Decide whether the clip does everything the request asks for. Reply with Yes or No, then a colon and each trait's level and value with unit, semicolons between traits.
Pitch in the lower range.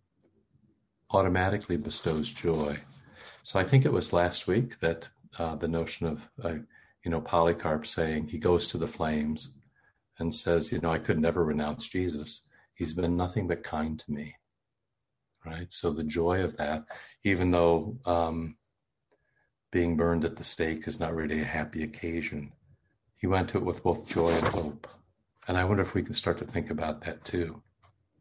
Yes: very low, 85 Hz